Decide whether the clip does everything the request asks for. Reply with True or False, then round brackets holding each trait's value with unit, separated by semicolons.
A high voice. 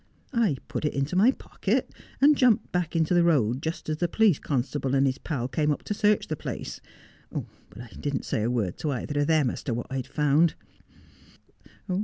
False (150 Hz)